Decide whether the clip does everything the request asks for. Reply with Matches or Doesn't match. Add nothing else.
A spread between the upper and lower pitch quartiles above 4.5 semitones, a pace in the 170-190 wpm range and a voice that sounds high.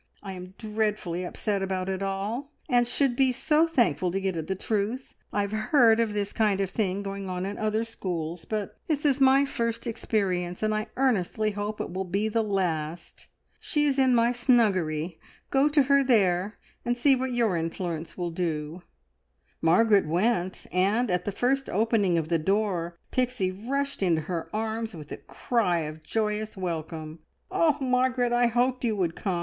Matches